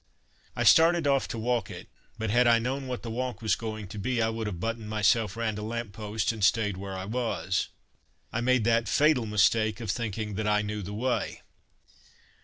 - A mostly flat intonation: Yes, narrow, 2.2 semitones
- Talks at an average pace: No, fast, 210 wpm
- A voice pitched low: Yes, low, 110 Hz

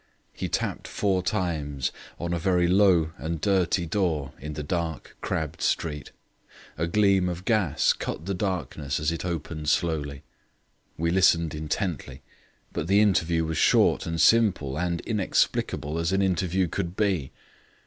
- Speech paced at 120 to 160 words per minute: Yes, average, 150 wpm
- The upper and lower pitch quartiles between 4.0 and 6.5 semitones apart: No, average, 3.3 semitones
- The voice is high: No, very low, 85 Hz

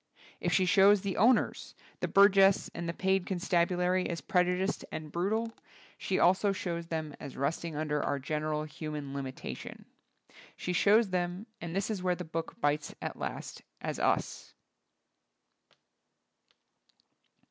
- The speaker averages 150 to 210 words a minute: No, average, 140 wpm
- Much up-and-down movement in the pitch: No, average, 3.7 semitones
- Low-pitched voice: No, medium, 175 Hz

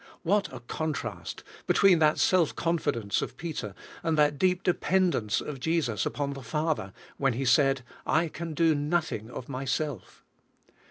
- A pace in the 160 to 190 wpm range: No, average, 150 wpm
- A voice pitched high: No, medium, 150 Hz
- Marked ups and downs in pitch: No, average, 4.3 semitones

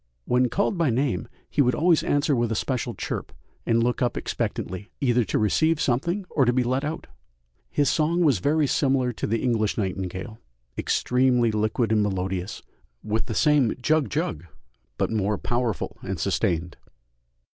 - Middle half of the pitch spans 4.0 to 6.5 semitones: Yes, average, 4.8 semitones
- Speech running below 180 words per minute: Yes, average, 165 wpm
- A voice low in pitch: Yes, low, 125 Hz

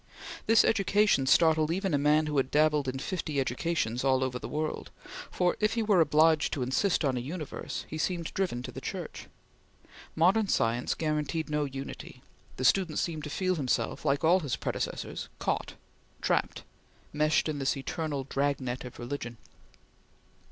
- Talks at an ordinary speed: Yes, average, 165 wpm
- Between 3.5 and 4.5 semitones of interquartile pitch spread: Yes, average, 4.0 semitones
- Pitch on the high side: No, medium, 150 Hz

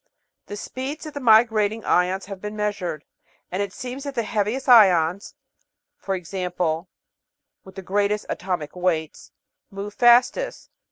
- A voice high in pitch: Yes, high, 200 Hz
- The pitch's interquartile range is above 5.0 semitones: No, average, 4.2 semitones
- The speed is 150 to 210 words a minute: No, slow, 135 wpm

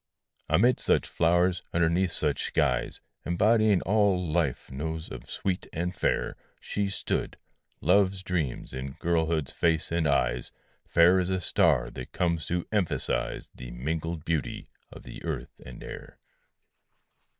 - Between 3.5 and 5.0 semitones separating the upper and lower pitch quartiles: No, average, 3.0 semitones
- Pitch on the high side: No, very low, 85 Hz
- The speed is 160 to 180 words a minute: No, slow, 135 wpm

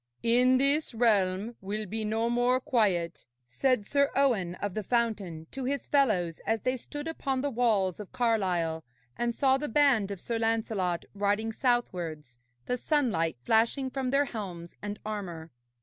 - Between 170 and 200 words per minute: No, average, 160 wpm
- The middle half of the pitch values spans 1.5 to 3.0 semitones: No, average, 5.1 semitones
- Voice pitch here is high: Yes, high, 225 Hz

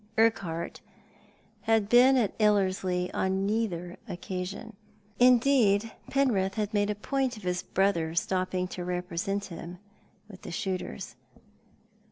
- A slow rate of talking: Yes, slow, 120 wpm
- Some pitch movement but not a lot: Yes, average, 3.6 semitones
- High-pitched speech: Yes, high, 195 Hz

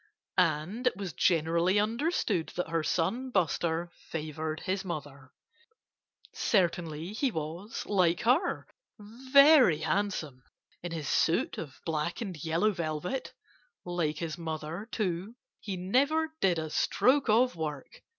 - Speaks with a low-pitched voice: No, medium, 175 Hz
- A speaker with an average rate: No, slow, 125 wpm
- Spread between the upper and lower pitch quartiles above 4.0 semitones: Yes, average, 5.2 semitones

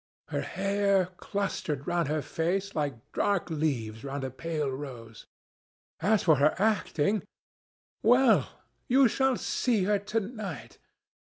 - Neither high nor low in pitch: Yes, medium, 180 Hz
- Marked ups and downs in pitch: Yes, wide, 6.1 semitones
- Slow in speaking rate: Yes, slow, 120 wpm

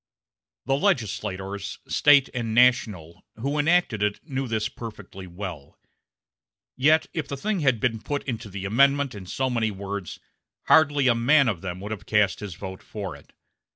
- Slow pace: No, average, 165 wpm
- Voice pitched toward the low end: Yes, low, 110 Hz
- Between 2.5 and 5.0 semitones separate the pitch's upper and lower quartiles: No, wide, 5.6 semitones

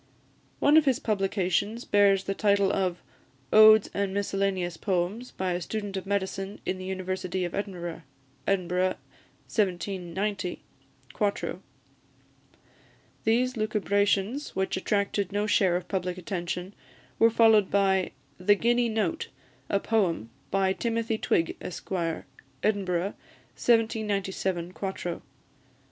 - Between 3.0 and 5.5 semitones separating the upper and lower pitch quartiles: No, narrow, 2.4 semitones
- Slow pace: Yes, slow, 115 wpm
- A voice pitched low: No, high, 195 Hz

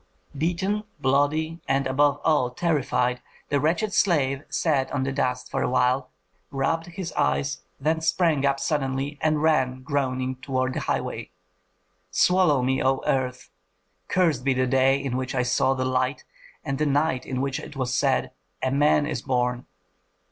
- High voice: No, low, 135 Hz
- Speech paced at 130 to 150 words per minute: No, average, 160 wpm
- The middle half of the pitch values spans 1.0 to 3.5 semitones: Yes, average, 2.8 semitones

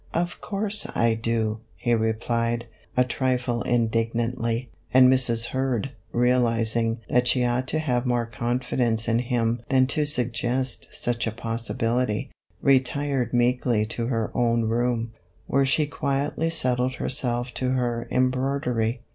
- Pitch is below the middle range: Yes, low, 120 Hz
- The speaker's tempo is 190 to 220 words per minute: No, average, 140 wpm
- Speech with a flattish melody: Yes, narrow, 1.9 semitones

